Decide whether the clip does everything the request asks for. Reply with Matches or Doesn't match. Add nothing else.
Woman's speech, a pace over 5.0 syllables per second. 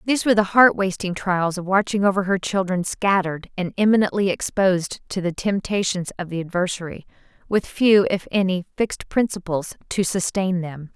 Matches